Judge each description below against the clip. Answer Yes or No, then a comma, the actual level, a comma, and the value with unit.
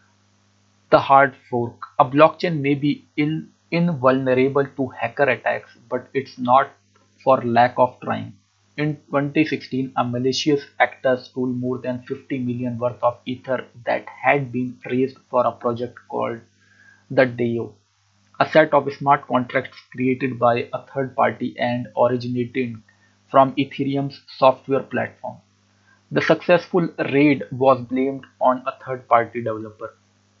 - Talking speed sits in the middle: No, slow, 130 wpm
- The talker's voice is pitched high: No, low, 130 Hz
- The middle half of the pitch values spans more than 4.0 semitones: No, narrow, 2.5 semitones